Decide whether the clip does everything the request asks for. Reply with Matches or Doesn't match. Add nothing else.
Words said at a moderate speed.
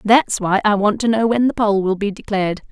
Doesn't match